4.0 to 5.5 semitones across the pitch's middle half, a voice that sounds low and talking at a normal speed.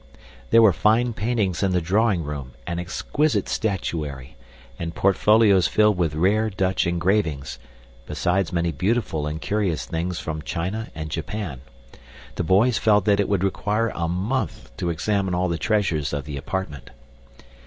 Yes: average, 4.5 semitones; very low, 90 Hz; average, 155 wpm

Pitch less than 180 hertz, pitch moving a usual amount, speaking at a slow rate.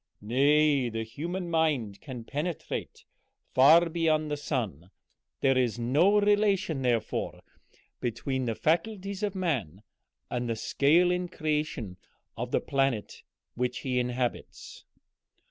No: medium, 140 Hz; wide, 5.7 semitones; slow, 120 wpm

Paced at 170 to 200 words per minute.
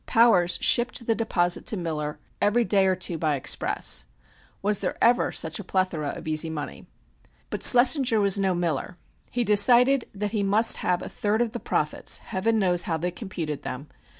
Yes: average, 180 wpm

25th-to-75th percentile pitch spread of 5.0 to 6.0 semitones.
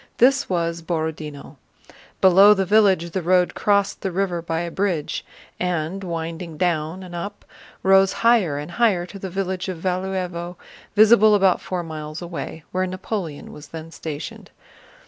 No: average, 2.7 semitones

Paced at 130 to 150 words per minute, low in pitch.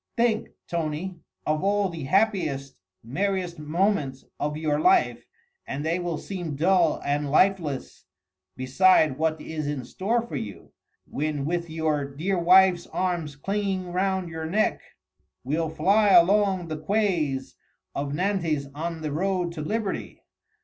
No: slow, 135 wpm; medium, 170 Hz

